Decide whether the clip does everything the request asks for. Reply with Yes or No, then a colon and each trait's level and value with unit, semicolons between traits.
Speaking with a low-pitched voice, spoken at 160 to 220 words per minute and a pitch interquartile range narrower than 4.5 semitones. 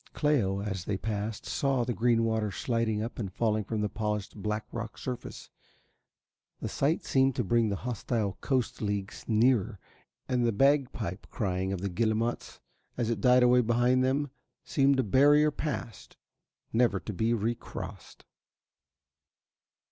No: low, 115 Hz; average, 150 wpm; average, 3.1 semitones